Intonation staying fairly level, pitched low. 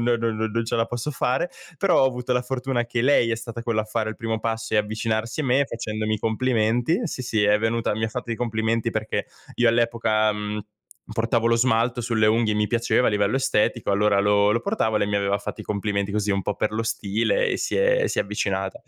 Yes: narrow, 2.3 semitones; low, 115 Hz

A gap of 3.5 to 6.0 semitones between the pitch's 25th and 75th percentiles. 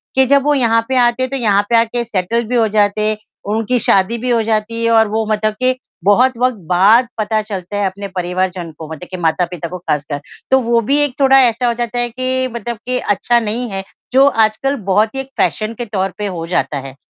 Yes: average, 3.8 semitones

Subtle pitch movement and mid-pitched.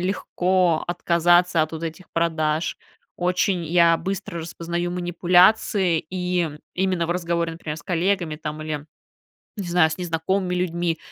Yes: narrow, 1.7 semitones; medium, 175 Hz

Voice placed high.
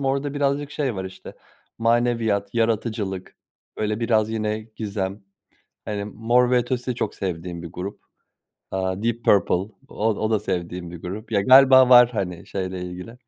No: low, 110 Hz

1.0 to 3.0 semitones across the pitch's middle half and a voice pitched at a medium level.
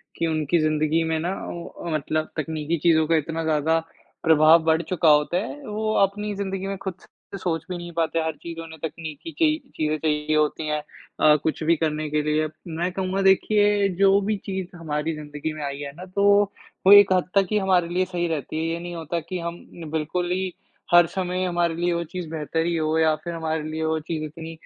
Yes: average, 2.7 semitones; medium, 165 Hz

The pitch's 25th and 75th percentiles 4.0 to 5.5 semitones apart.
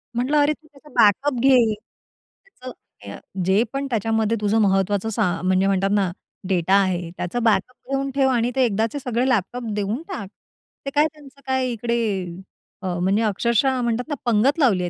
Yes: average, 5.0 semitones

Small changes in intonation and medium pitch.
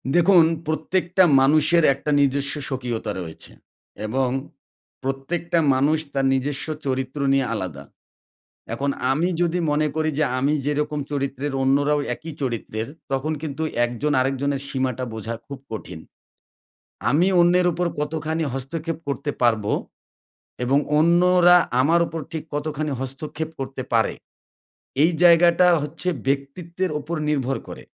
No: average, 3.4 semitones; medium, 145 Hz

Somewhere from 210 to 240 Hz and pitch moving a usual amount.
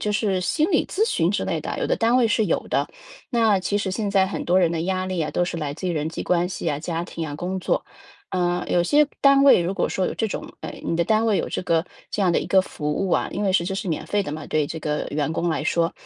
No: medium, 185 Hz; average, 3.7 semitones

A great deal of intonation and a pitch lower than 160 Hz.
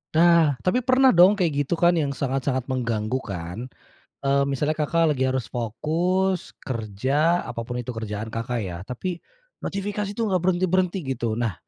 Yes: wide, 6.9 semitones; medium, 140 Hz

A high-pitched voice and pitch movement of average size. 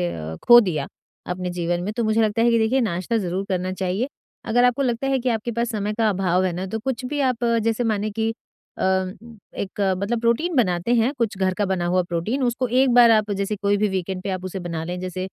Yes: high, 210 Hz; average, 4.2 semitones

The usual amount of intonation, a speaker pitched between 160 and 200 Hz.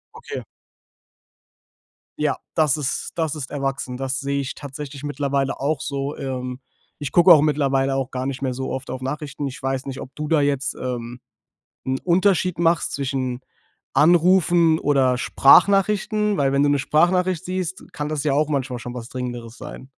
No: average, 3.0 semitones; medium, 140 Hz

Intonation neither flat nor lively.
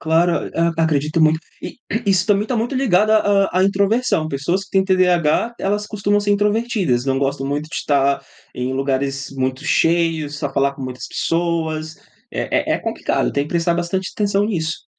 No: wide, 5.7 semitones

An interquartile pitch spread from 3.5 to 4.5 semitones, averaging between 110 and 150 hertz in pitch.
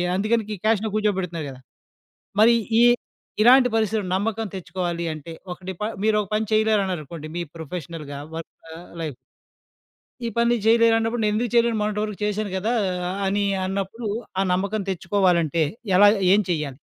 No: average, 4.1 semitones; high, 205 Hz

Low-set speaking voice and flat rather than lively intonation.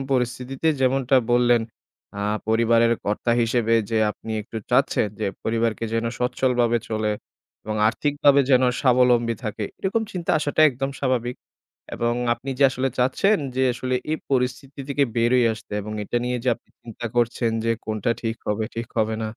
Yes: low, 120 Hz; narrow, 2.3 semitones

